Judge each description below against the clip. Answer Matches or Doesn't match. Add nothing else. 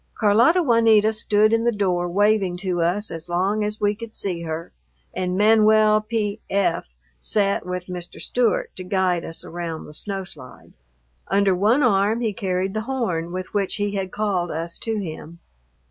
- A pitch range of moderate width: Matches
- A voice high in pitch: Matches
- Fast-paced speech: Doesn't match